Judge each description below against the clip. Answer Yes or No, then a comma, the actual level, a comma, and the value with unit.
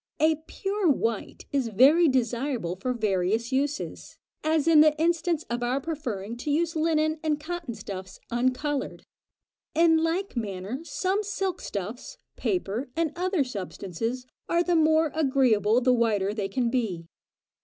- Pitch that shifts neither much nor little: No, wide, 6.0 semitones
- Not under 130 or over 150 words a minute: Yes, average, 145 wpm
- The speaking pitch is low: No, very high, 270 Hz